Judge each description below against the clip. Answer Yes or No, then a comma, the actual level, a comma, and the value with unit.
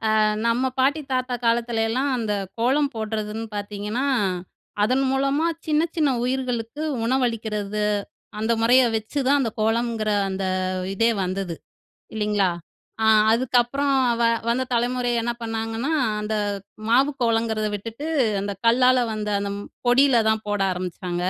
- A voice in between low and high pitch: No, high, 230 Hz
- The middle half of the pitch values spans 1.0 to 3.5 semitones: Yes, average, 3.2 semitones